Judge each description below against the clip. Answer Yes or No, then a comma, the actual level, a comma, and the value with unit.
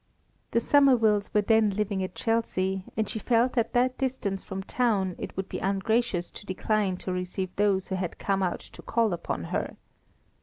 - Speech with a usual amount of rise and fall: Yes, average, 3.3 semitones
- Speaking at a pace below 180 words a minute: No, average, 185 wpm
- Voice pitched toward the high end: Yes, high, 205 Hz